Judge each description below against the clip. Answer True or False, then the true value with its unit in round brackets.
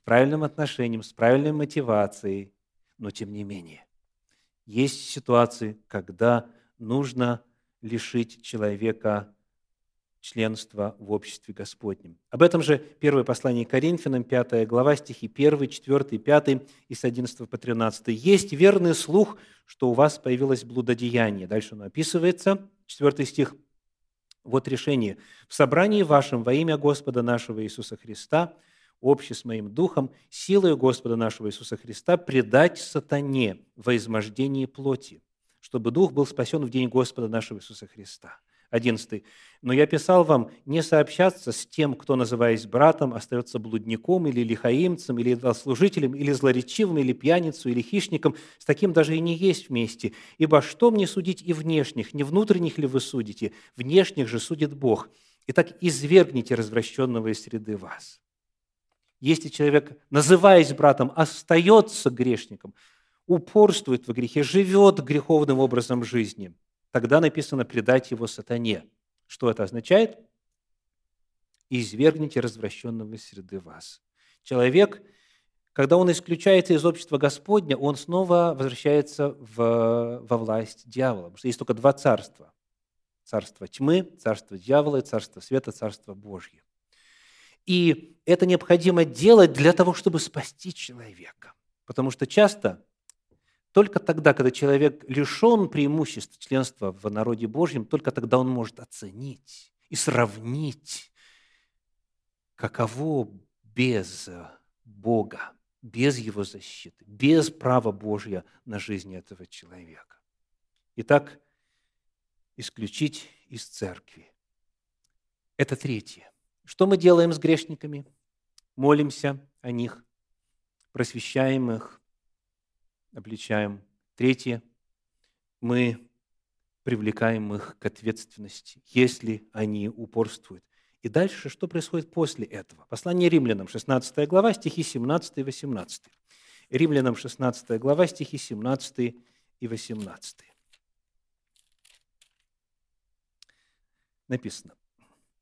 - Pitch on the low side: True (125 Hz)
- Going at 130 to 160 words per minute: False (115 wpm)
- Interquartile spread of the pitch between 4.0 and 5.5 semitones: True (5.1 semitones)